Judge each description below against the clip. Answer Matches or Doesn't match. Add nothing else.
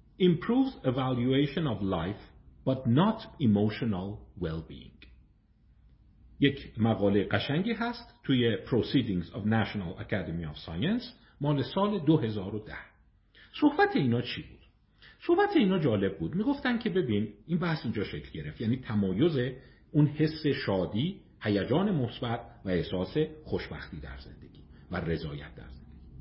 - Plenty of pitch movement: Matches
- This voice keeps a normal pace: Matches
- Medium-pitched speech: Doesn't match